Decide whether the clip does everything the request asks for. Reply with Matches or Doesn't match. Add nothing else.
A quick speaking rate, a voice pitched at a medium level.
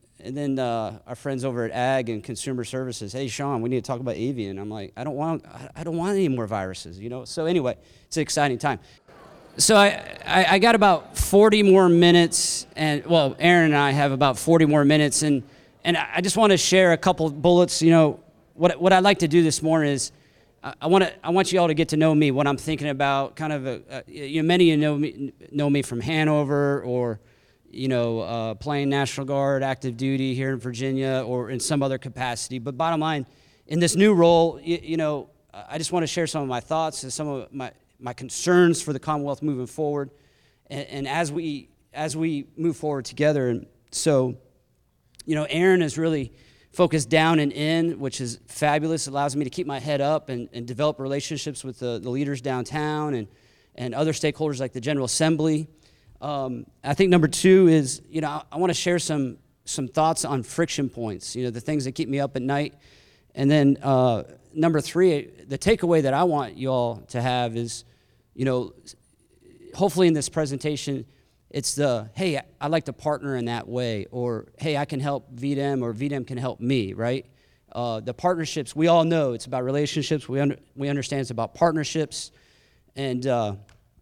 Matches